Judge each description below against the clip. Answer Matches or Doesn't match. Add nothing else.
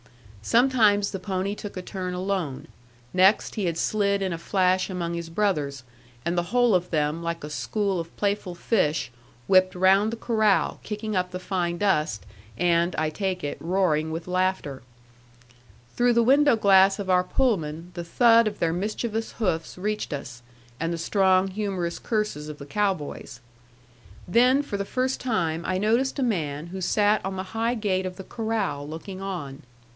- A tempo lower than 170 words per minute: Doesn't match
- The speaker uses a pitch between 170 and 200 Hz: Matches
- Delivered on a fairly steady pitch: Doesn't match